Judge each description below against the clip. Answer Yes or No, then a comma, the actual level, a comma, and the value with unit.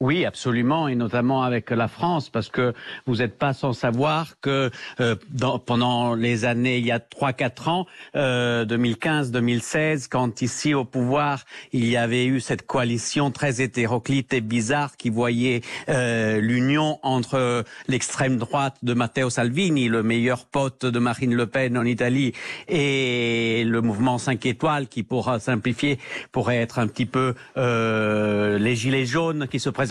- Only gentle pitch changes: Yes, narrow, 2.3 semitones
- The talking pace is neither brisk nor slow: Yes, average, 160 wpm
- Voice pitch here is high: No, low, 125 Hz